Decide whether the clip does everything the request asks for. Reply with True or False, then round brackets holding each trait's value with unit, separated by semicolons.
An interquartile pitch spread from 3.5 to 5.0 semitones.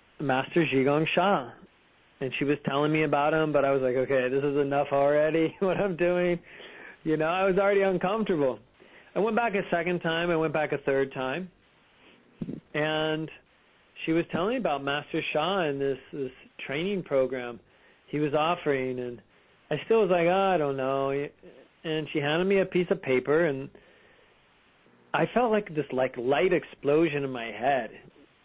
True (4.5 semitones)